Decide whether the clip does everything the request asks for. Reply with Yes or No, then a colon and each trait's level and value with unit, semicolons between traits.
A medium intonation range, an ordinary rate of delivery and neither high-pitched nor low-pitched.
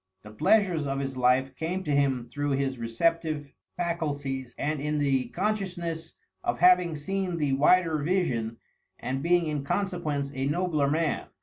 Yes: average, 4.1 semitones; average, 150 wpm; medium, 150 Hz